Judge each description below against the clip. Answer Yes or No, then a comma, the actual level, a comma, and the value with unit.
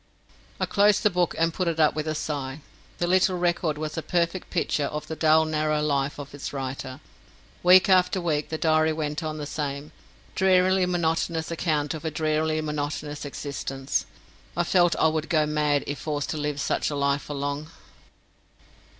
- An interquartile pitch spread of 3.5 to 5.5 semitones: No, narrow, 2.4 semitones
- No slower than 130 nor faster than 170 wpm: No, average, 185 wpm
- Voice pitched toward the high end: No, medium, 155 Hz